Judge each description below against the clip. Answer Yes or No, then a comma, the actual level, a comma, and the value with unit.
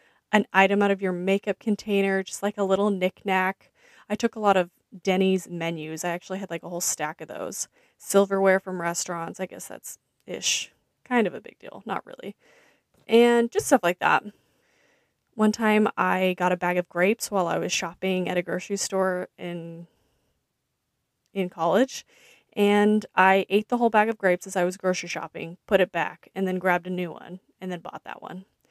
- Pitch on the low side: No, high, 190 Hz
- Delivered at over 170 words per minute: Yes, average, 195 wpm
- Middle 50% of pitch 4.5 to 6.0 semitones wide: No, average, 2.7 semitones